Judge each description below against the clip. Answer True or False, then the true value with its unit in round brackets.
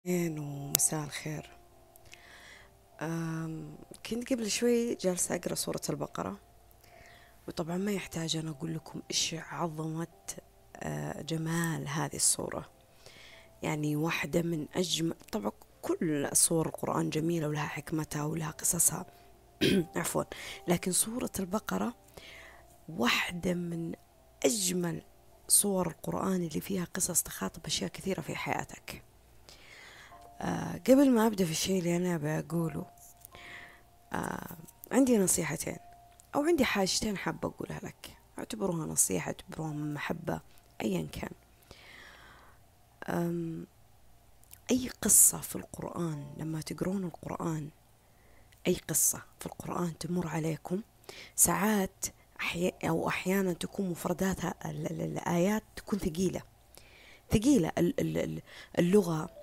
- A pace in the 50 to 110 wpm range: True (100 wpm)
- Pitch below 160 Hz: False (170 Hz)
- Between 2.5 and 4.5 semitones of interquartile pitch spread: True (3.3 semitones)